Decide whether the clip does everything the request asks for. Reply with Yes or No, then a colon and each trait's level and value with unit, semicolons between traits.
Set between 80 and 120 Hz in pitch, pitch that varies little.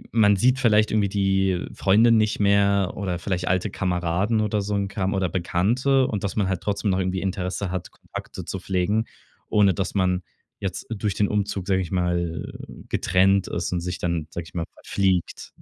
Yes: very low, 95 Hz; narrow, 2.2 semitones